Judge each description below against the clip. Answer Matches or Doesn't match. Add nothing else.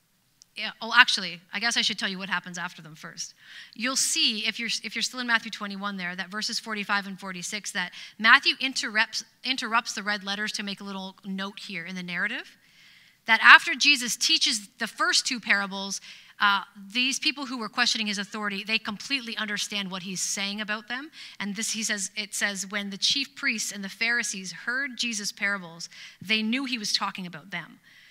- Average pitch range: Matches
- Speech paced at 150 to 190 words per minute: Doesn't match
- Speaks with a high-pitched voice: Matches